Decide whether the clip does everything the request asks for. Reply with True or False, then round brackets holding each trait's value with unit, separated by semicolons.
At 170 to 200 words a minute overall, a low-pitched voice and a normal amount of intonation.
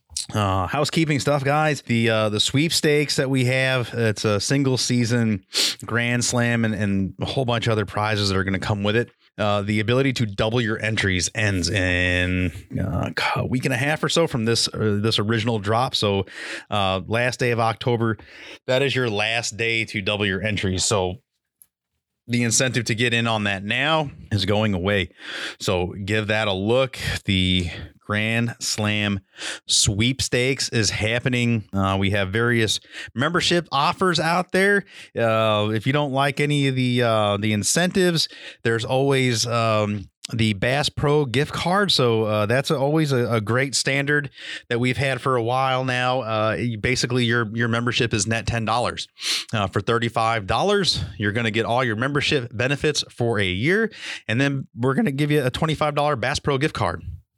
True (180 wpm; 115 Hz; 4.0 semitones)